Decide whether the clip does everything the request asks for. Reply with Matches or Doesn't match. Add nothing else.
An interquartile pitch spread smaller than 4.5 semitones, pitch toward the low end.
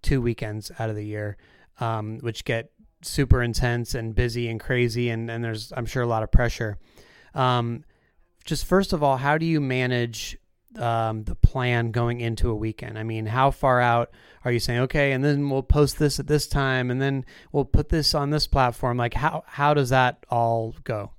Matches